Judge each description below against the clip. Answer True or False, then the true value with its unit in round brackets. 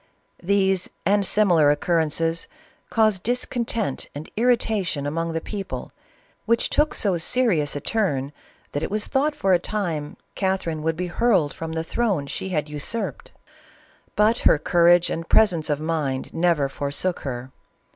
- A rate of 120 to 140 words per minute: False (155 wpm)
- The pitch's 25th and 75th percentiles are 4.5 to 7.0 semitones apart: True (5.5 semitones)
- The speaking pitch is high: False (175 Hz)